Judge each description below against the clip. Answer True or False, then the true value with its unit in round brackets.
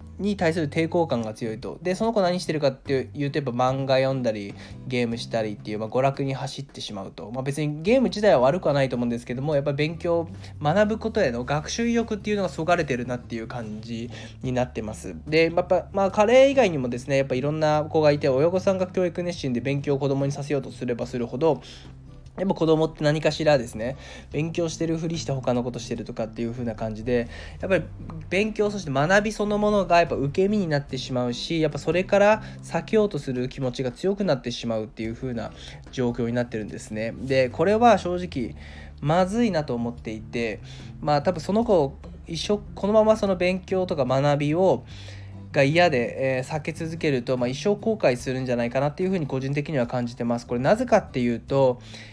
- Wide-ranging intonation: True (6.4 semitones)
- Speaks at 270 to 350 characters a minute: False (435 characters per minute)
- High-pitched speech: False (140 Hz)